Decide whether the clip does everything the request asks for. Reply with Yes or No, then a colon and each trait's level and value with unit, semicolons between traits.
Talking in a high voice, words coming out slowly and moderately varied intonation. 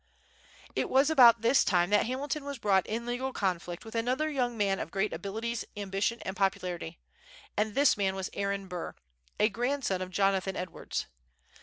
No: high, 210 Hz; average, 170 wpm; average, 4.1 semitones